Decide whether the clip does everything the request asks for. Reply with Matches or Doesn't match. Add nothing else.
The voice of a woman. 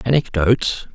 Doesn't match